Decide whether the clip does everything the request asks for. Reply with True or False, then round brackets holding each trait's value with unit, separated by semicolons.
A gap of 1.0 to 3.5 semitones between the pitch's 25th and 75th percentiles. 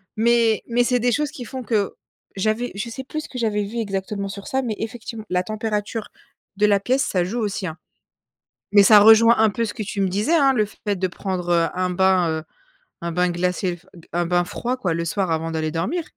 False (4.2 semitones)